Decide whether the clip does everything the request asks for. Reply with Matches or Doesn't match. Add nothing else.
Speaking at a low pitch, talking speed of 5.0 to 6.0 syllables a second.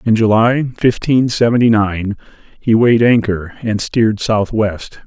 Doesn't match